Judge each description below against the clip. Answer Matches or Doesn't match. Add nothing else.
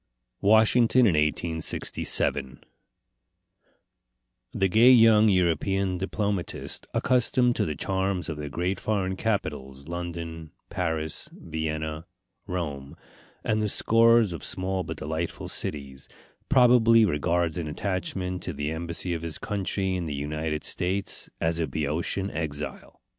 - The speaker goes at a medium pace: Doesn't match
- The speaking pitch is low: Matches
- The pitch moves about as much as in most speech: Matches